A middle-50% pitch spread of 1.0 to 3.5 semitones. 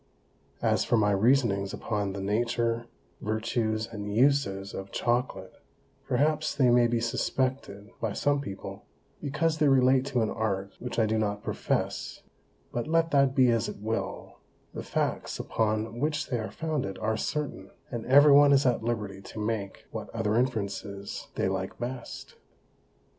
No: average, 4.3 semitones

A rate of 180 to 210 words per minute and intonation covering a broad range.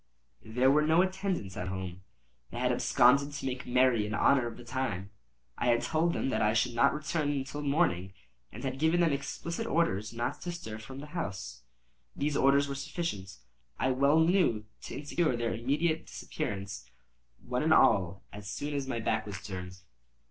Yes: average, 185 wpm; wide, 5.9 semitones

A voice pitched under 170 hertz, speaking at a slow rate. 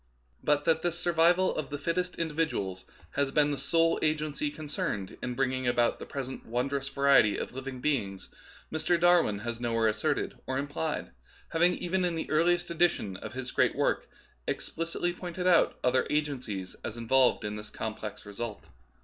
No: medium, 140 Hz; average, 165 wpm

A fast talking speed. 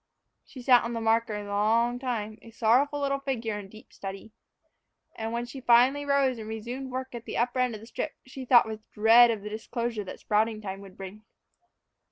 Yes: fast, 210 wpm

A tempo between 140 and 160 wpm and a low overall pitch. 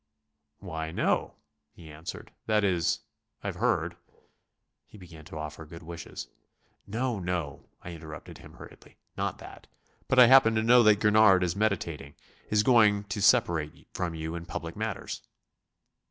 Yes: average, 150 wpm; very low, 90 Hz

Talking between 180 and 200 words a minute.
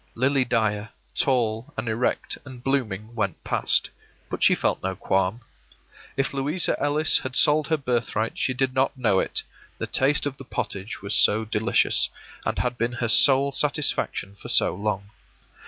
No: average, 165 wpm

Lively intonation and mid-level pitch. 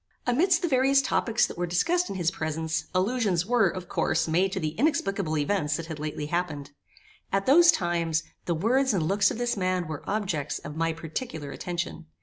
Yes: wide, 6.3 semitones; medium, 180 Hz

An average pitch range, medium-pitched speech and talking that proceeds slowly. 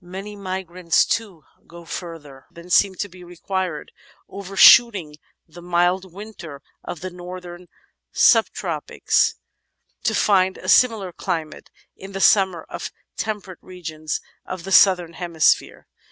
No: narrow, 2.2 semitones; medium, 180 Hz; slow, 125 wpm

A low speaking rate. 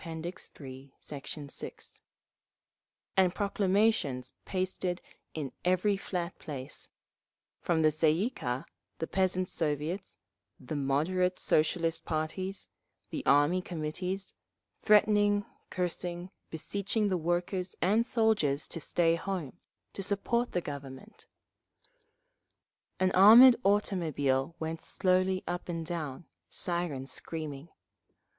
Yes: slow, 100 wpm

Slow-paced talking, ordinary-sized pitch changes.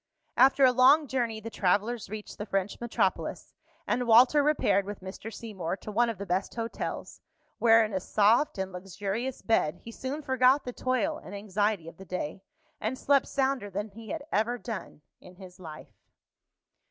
No: average, 175 wpm; average, 4.5 semitones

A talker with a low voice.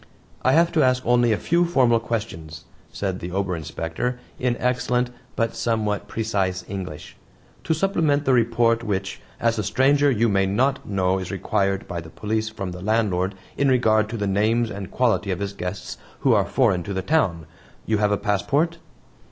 Yes: low, 110 Hz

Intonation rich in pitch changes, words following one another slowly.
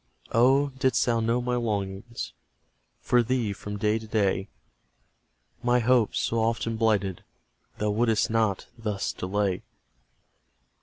No: average, 2.7 semitones; slow, 120 wpm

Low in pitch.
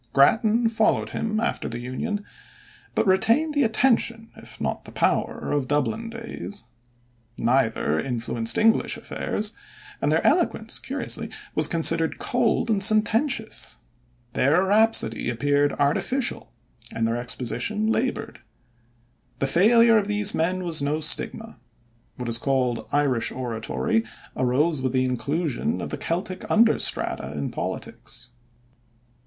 No: medium, 170 Hz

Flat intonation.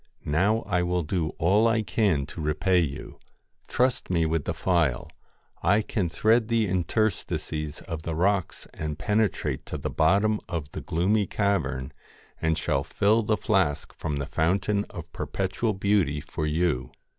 No: average, 5.1 semitones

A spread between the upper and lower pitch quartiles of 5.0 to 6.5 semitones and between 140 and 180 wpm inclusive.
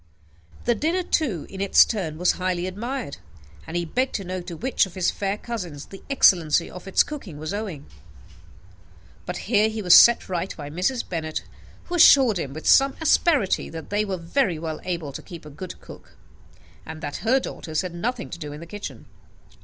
No: wide, 5.5 semitones; average, 195 wpm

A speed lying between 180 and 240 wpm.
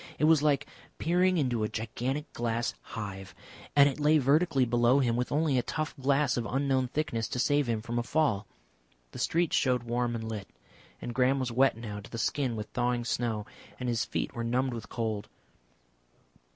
Yes: average, 190 wpm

